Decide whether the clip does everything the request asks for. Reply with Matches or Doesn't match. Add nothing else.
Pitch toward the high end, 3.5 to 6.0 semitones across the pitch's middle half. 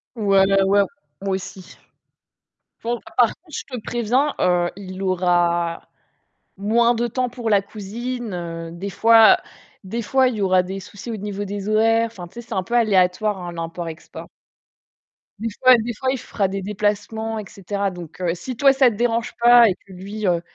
Matches